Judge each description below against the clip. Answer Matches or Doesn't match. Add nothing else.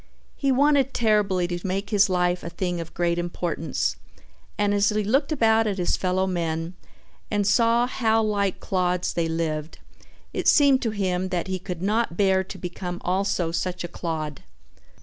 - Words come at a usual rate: Matches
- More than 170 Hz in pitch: Matches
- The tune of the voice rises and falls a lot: Doesn't match